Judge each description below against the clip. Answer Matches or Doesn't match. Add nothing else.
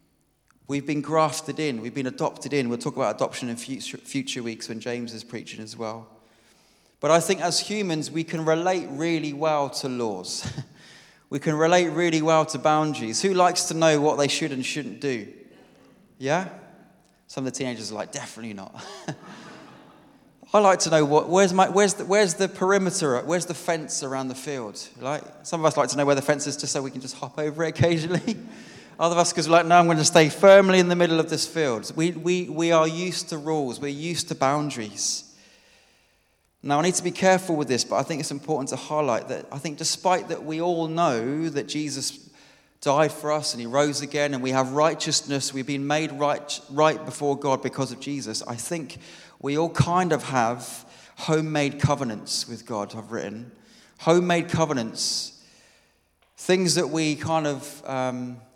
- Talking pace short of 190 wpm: Doesn't match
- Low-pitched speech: Doesn't match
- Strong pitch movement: Doesn't match